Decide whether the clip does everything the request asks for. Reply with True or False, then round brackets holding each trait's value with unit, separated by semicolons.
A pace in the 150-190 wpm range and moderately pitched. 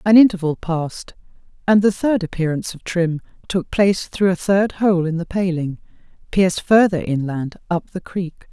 True (170 wpm; 180 Hz)